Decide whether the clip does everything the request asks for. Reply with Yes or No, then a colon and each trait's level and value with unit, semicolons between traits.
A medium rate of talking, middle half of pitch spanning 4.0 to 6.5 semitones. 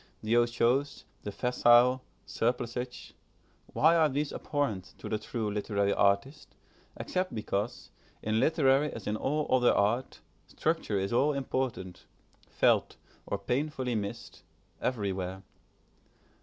No: slow, 115 wpm; average, 4.7 semitones